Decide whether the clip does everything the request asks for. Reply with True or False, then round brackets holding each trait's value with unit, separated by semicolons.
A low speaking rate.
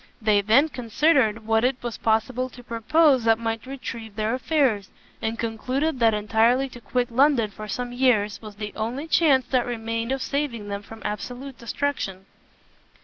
False (165 wpm)